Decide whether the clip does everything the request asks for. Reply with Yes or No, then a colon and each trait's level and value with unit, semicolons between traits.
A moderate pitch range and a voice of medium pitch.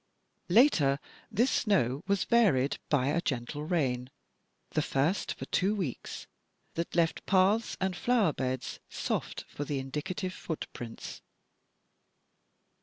No: wide, 6.4 semitones; medium, 165 Hz